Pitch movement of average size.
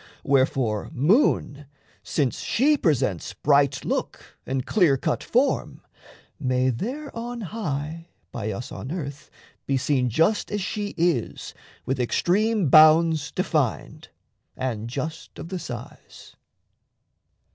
No: wide, 6.6 semitones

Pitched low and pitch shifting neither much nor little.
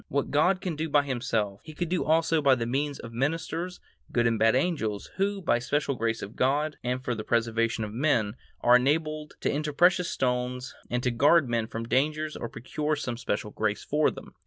Yes: low, 130 Hz; average, 4.8 semitones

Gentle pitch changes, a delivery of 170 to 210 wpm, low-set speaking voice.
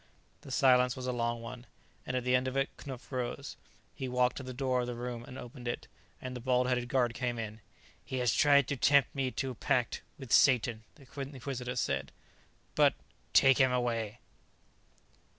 Yes: narrow, 1.4 semitones; average, 195 wpm; low, 125 Hz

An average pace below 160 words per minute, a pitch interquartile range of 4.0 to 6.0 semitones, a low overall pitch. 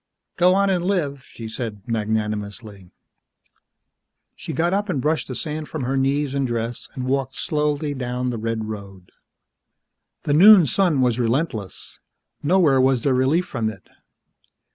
Yes: average, 150 wpm; average, 5.2 semitones; low, 130 Hz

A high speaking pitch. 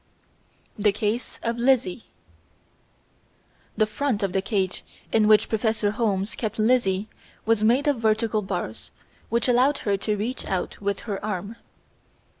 Yes: high, 215 Hz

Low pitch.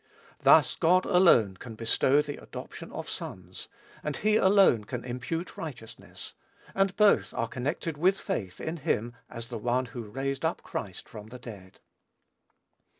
Yes: low, 130 Hz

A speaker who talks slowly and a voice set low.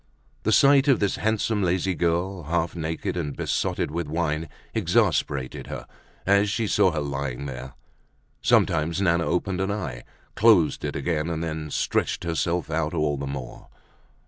No: average, 155 wpm; very low, 85 Hz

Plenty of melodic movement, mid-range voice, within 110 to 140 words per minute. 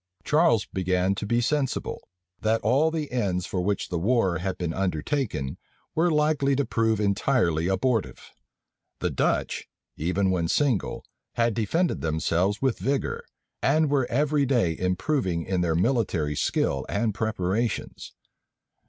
No: wide, 6.9 semitones; low, 110 Hz; slow, 135 wpm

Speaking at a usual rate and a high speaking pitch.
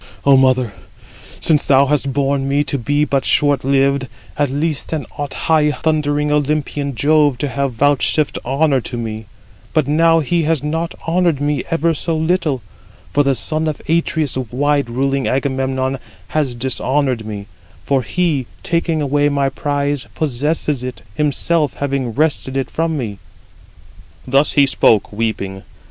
No: average, 150 wpm; medium, 140 Hz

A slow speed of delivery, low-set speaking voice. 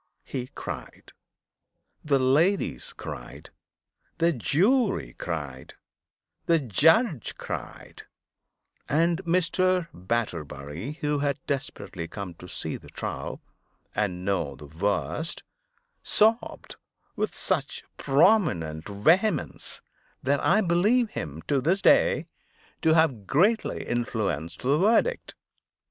No: slow, 100 wpm; medium, 145 Hz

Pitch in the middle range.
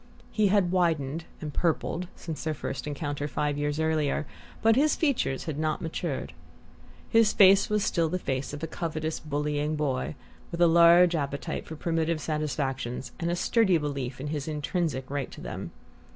Yes: medium, 155 Hz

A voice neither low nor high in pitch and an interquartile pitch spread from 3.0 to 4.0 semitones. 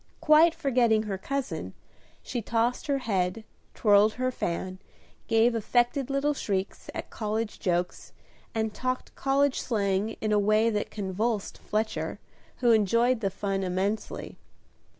No: high, 220 Hz; average, 3.6 semitones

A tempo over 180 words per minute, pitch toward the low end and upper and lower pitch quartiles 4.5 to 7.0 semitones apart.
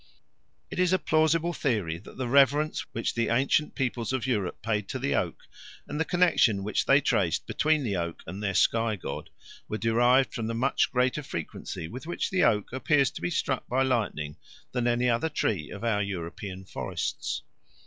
Yes: average, 190 wpm; low, 120 Hz; average, 5.0 semitones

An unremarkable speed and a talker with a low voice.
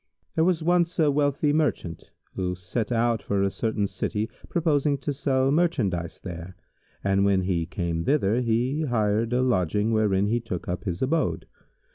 Yes: average, 170 wpm; low, 115 Hz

